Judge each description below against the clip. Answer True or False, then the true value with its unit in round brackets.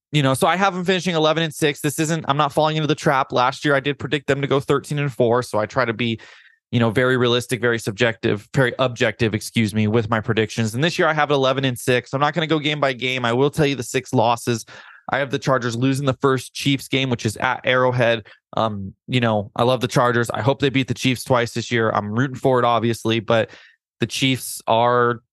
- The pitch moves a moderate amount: True (3.2 semitones)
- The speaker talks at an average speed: False (255 wpm)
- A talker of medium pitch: False (130 Hz)